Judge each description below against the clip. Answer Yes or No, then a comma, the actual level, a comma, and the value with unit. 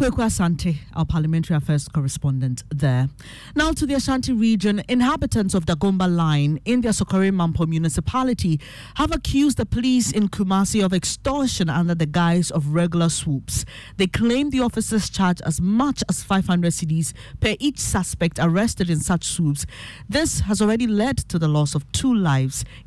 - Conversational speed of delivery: Yes, average, 160 wpm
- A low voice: No, medium, 175 Hz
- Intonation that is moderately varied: No, wide, 5.9 semitones